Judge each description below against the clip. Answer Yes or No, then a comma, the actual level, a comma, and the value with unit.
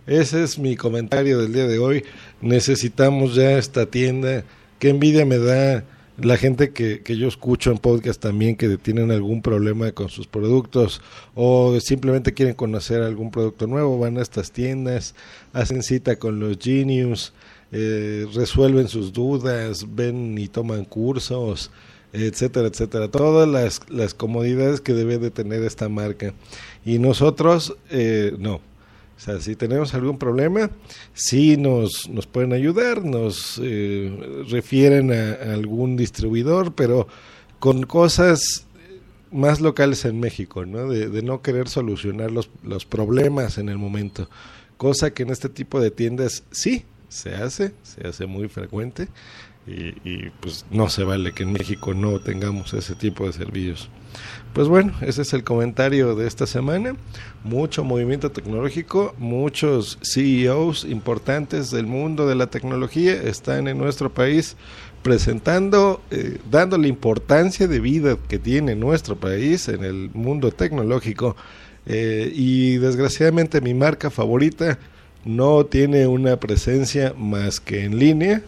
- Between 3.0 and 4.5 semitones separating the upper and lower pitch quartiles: Yes, average, 4.0 semitones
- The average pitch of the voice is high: No, low, 120 Hz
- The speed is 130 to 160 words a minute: Yes, average, 145 wpm